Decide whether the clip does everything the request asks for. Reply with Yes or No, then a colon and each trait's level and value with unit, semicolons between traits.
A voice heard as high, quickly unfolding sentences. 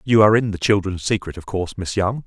No: low, 100 Hz; fast, 265 wpm